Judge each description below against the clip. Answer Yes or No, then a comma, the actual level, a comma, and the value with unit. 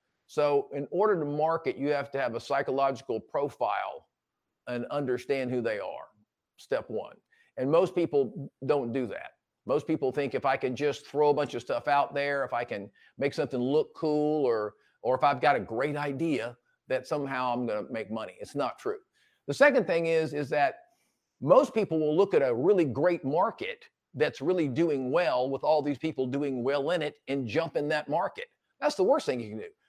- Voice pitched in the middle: Yes, medium, 145 Hz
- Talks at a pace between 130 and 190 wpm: No, fast, 205 wpm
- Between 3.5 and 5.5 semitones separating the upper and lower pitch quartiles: Yes, average, 4.2 semitones